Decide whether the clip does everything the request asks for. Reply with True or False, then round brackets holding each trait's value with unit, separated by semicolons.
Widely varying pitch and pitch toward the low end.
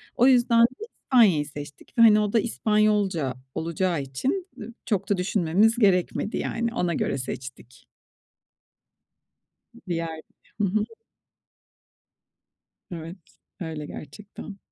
False (5.7 semitones; 195 Hz)